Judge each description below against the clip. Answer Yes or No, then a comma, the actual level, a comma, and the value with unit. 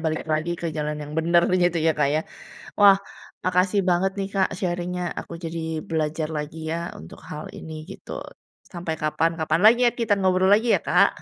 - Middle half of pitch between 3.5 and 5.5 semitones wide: No, average, 2.8 semitones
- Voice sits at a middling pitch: Yes, medium, 170 Hz